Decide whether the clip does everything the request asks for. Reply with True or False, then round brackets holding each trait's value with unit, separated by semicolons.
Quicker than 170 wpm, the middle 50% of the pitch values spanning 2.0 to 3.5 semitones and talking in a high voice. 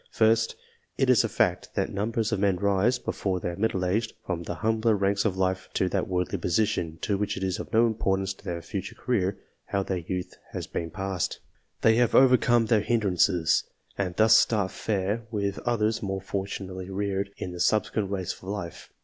False (185 wpm; 2.8 semitones; 100 Hz)